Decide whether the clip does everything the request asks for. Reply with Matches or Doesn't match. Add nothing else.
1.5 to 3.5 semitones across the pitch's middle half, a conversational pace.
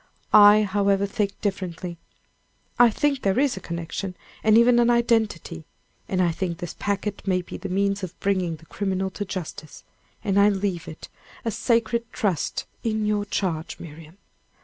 Matches